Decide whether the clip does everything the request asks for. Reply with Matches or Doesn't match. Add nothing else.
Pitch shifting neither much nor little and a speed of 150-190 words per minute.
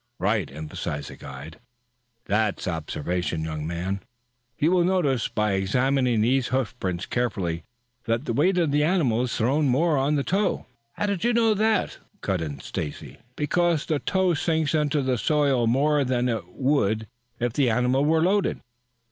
Doesn't match